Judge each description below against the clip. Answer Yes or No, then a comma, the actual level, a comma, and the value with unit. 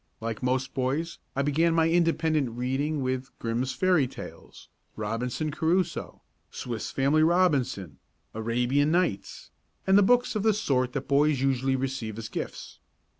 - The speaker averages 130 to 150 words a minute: Yes, slow, 135 wpm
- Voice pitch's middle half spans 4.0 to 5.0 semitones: Yes, average, 4.4 semitones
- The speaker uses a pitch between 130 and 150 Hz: Yes, low, 135 Hz